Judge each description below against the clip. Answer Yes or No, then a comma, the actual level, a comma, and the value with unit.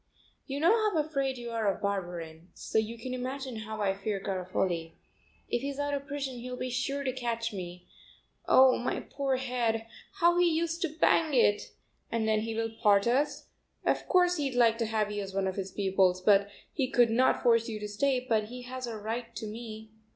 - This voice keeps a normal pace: No, fast, 210 wpm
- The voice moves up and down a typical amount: Yes, average, 4.3 semitones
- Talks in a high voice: Yes, high, 235 Hz